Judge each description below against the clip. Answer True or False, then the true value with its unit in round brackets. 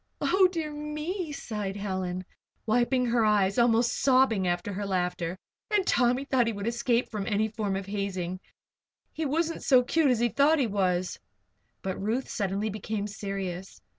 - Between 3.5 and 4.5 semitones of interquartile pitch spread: False (5.0 semitones)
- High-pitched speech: True (220 Hz)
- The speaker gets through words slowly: False (165 wpm)